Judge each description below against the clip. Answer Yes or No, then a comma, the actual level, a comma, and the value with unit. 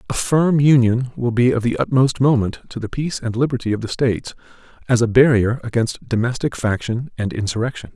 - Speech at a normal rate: Yes, average, 190 wpm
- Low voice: Yes, low, 120 Hz